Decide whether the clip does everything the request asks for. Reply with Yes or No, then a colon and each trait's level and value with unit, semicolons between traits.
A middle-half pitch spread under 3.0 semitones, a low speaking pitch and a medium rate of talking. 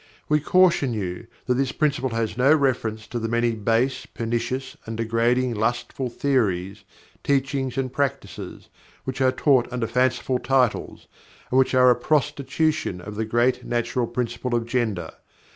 Yes: narrow, 2.6 semitones; low, 125 Hz; average, 150 wpm